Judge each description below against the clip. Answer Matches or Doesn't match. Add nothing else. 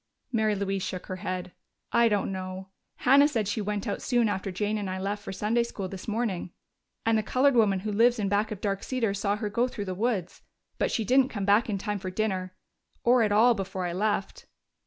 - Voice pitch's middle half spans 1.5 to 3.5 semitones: Matches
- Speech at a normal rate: Doesn't match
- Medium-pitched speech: Doesn't match